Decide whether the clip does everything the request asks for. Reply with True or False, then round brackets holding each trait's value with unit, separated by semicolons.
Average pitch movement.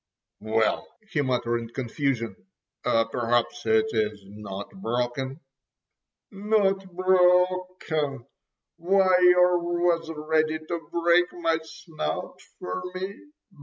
False (6.9 semitones)